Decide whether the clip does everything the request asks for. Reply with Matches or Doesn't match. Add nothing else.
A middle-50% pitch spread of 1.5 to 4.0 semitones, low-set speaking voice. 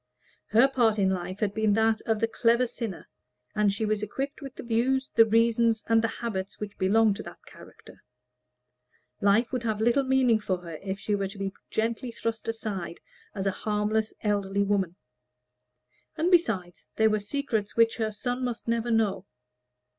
Doesn't match